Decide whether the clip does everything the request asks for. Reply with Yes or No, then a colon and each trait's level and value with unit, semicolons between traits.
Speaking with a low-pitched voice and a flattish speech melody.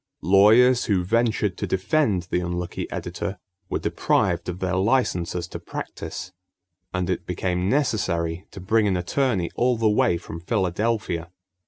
No: very low, 95 Hz; average, 4.3 semitones